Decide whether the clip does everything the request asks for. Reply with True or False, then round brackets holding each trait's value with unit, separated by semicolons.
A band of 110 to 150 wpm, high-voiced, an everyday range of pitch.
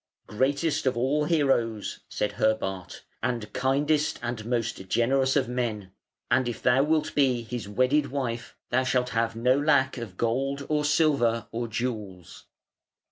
False (145 wpm; 125 Hz; 3.4 semitones)